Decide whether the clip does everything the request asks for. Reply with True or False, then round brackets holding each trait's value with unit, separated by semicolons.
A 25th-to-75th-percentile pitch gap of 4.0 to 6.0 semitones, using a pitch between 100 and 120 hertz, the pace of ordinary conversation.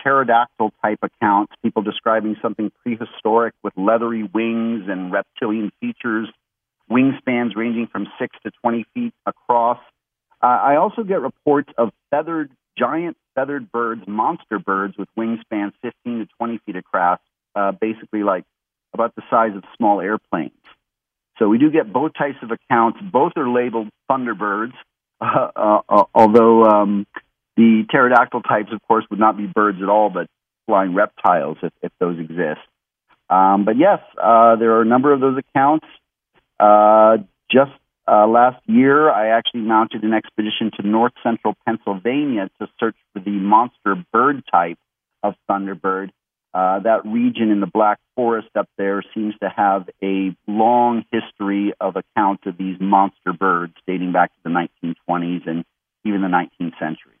False (2.6 semitones; 110 Hz; 155 wpm)